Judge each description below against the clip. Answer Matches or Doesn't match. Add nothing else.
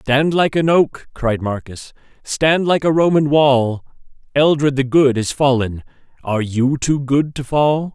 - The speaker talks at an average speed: Matches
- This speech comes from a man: Matches